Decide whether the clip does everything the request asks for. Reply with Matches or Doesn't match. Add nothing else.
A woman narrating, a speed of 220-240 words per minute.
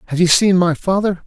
Doesn't match